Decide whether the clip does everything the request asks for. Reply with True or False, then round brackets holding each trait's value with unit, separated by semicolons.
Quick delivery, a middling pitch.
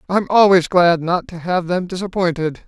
False (180 wpm; 180 Hz)